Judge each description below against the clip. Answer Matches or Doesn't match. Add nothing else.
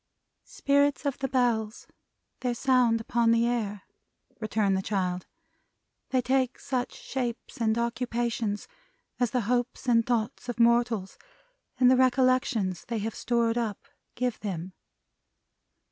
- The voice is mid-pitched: Doesn't match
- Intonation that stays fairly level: Matches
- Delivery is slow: Matches